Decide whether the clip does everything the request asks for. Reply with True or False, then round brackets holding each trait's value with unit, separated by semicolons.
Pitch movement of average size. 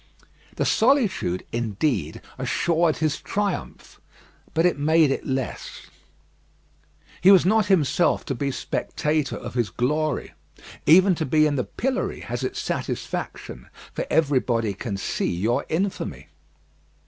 False (6.4 semitones)